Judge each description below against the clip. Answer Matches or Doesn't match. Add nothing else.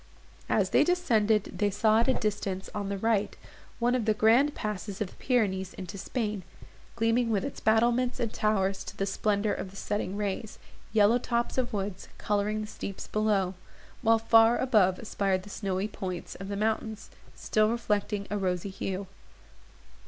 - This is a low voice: Doesn't match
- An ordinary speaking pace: Matches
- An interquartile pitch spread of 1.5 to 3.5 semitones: Matches